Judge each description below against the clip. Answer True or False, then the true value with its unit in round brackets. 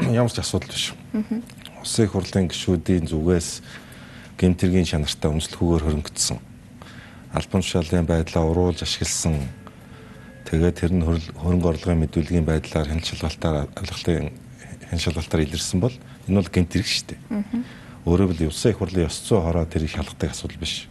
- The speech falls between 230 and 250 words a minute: False (140 wpm)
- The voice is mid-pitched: False (85 Hz)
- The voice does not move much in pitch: False (3.2 semitones)